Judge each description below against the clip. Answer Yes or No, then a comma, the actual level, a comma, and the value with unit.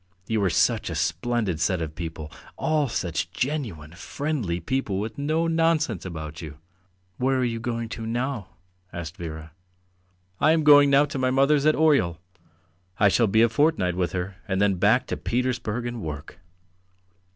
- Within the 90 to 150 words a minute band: No, average, 170 wpm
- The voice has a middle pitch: No, low, 115 Hz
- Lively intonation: Yes, wide, 7.6 semitones